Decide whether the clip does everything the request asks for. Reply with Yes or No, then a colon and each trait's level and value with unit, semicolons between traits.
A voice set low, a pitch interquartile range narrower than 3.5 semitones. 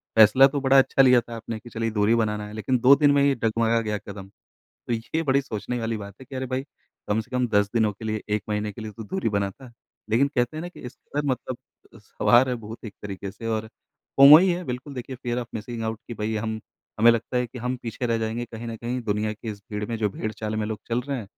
Yes: low, 115 Hz; average, 2.9 semitones